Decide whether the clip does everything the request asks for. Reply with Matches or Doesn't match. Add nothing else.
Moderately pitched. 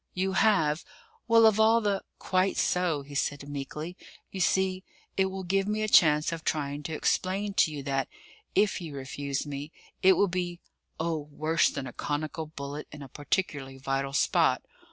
Matches